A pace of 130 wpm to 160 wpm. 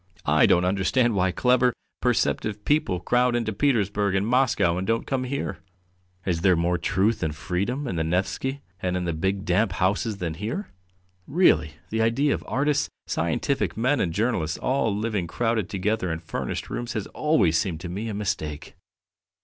No: average, 175 wpm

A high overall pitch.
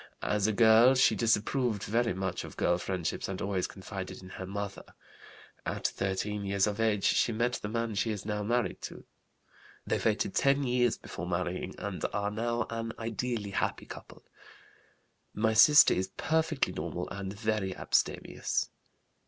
No: low, 105 Hz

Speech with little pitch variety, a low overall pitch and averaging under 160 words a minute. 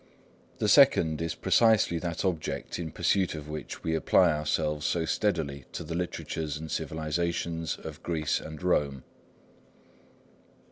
Yes: narrow, 2.0 semitones; very low, 80 Hz; slow, 135 wpm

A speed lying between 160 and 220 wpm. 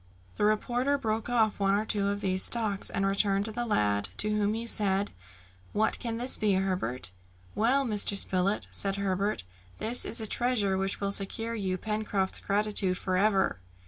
Yes: average, 175 wpm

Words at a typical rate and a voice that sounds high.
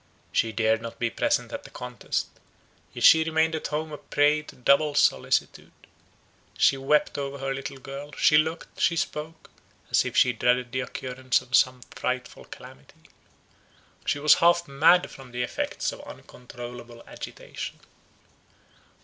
No: average, 150 wpm; low, 135 Hz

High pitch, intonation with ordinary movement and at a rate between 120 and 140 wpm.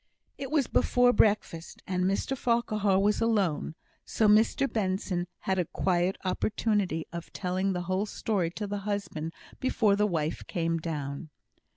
No: high, 195 Hz; average, 3.5 semitones; average, 150 wpm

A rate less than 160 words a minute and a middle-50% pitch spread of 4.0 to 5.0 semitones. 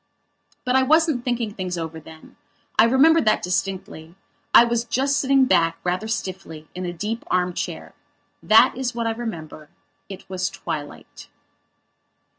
No: average, 150 wpm; wide, 5.4 semitones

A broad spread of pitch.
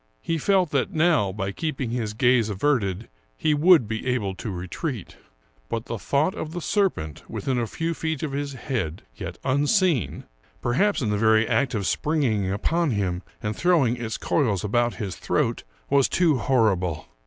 Yes: wide, 6.7 semitones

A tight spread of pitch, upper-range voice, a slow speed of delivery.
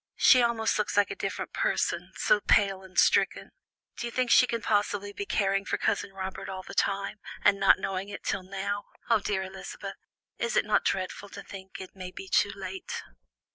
No: narrow, 1.4 semitones; high, 200 Hz; average, 200 wpm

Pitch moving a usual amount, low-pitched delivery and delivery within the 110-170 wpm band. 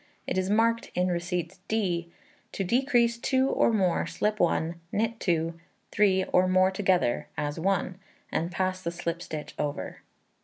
No: average, 3.7 semitones; medium, 185 Hz; average, 155 wpm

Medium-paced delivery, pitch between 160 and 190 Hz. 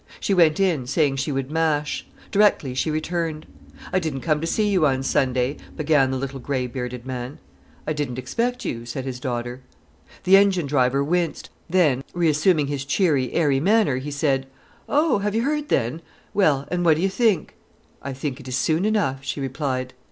No: average, 185 wpm; medium, 145 Hz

